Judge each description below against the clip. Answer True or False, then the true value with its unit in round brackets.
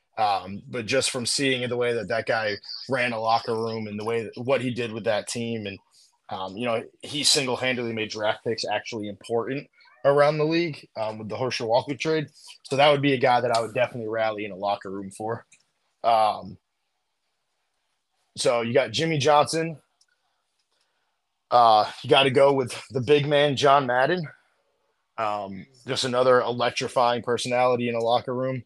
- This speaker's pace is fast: False (180 wpm)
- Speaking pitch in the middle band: False (125 Hz)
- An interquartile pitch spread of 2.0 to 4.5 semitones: True (3.7 semitones)